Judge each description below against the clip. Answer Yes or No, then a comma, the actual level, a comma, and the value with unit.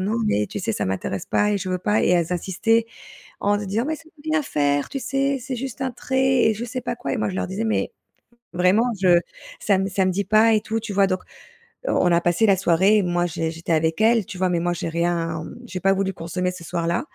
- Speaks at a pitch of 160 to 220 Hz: Yes, high, 190 Hz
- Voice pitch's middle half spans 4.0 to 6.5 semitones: Yes, average, 4.5 semitones